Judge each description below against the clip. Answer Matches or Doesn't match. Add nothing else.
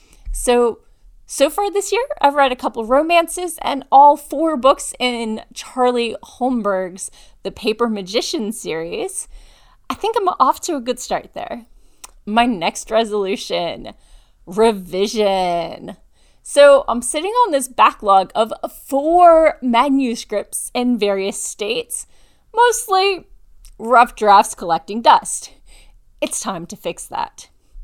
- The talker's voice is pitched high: Matches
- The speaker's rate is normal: Doesn't match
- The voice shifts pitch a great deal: Matches